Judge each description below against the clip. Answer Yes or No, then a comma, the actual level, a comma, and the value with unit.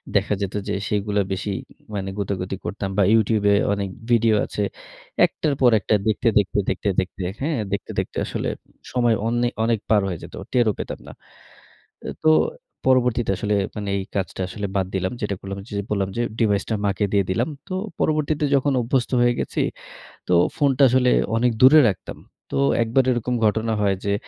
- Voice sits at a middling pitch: No, low, 105 Hz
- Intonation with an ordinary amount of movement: Yes, average, 3.6 semitones